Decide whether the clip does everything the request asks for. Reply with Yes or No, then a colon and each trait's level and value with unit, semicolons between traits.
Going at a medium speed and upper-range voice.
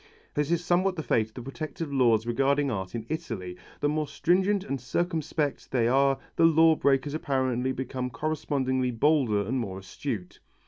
No: average, 170 wpm; low, 135 Hz